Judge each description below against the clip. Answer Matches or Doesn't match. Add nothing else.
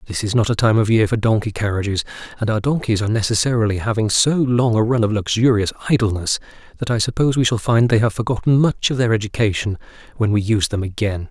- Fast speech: Matches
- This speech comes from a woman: Doesn't match